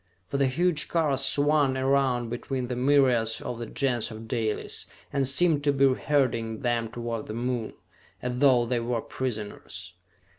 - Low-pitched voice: Yes, low, 125 Hz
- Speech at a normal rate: Yes, average, 160 wpm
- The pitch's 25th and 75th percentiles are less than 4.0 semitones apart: Yes, average, 3.1 semitones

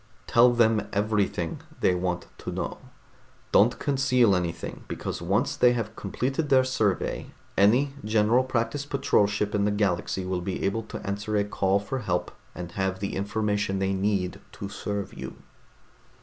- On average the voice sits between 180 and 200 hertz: No, low, 105 Hz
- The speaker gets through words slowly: No, average, 160 wpm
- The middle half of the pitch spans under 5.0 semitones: Yes, average, 3.3 semitones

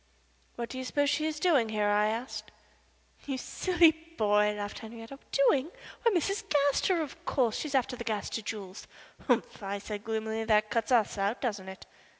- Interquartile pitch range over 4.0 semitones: Yes, average, 5.0 semitones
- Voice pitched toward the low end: No, high, 230 Hz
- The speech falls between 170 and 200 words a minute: Yes, average, 180 wpm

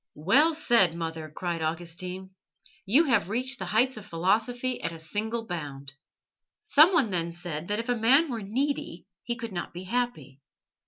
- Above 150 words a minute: Yes, average, 165 wpm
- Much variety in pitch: Yes, wide, 6.6 semitones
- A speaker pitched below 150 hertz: No, high, 205 Hz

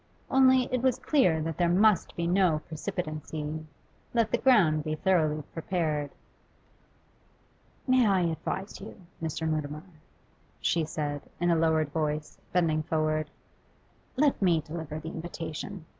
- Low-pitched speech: No, medium, 160 Hz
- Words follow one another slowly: Yes, slow, 130 wpm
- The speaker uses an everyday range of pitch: Yes, average, 3.5 semitones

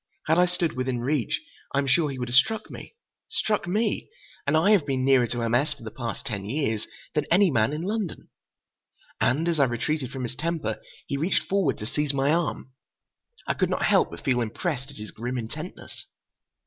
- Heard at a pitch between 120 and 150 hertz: Yes, medium, 140 Hz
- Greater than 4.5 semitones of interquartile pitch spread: Yes, average, 5.2 semitones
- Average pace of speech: No, fast, 210 wpm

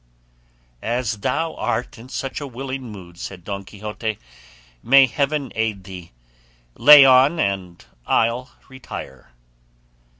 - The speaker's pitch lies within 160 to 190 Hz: No, low, 115 Hz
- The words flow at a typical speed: No, slow, 120 wpm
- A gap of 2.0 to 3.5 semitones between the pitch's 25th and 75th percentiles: No, average, 5.3 semitones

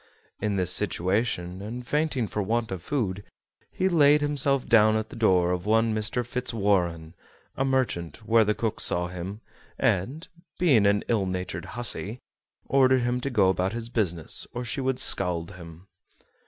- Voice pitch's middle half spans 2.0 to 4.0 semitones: No, average, 5.1 semitones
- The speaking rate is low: No, average, 165 wpm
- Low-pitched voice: Yes, low, 110 Hz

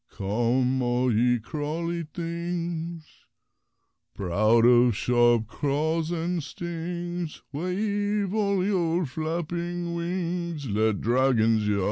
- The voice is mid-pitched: Yes, medium, 160 Hz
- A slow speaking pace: Yes, slow, 95 wpm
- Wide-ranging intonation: Yes, wide, 6.1 semitones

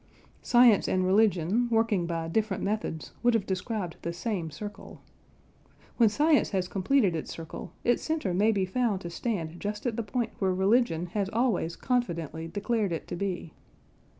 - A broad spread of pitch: No, average, 4.6 semitones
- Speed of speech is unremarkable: Yes, average, 165 wpm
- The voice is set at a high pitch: Yes, high, 200 Hz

